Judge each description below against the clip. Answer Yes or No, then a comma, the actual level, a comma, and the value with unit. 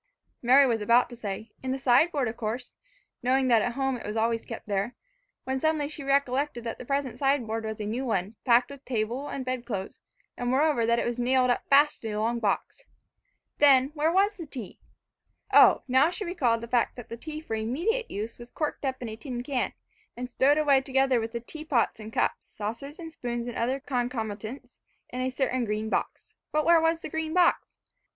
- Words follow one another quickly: Yes, fast, 210 wpm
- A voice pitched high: Yes, very high, 250 Hz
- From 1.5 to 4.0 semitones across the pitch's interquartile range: Yes, average, 3.4 semitones